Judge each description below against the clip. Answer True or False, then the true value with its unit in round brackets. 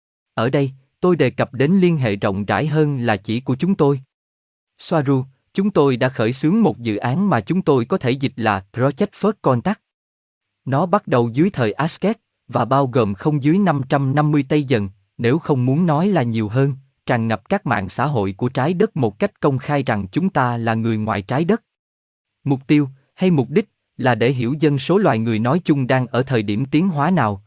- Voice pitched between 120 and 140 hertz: True (135 Hz)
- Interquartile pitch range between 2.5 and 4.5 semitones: False (5.5 semitones)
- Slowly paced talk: False (215 wpm)